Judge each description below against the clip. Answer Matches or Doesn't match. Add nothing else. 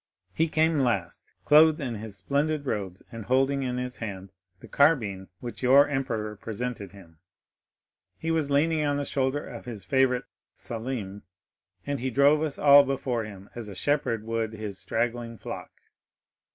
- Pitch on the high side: Doesn't match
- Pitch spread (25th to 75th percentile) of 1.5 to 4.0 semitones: Doesn't match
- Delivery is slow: Doesn't match